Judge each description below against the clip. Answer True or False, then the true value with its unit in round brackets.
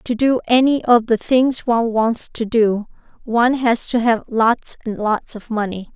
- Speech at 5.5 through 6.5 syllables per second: False (4.4 syllables/s)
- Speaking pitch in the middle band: False (230 Hz)